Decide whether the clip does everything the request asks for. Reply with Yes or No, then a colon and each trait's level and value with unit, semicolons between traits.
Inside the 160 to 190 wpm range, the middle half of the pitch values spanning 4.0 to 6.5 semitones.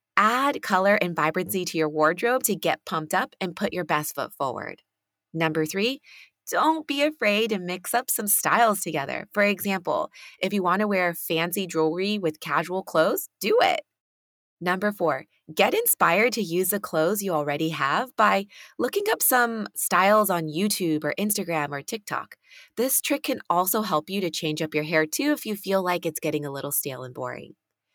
Yes: average, 185 wpm; average, 5.1 semitones